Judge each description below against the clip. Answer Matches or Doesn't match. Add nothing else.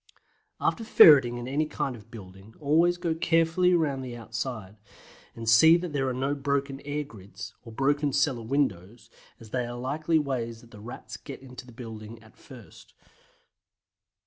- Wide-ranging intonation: Doesn't match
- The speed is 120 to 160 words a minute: Doesn't match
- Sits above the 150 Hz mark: Doesn't match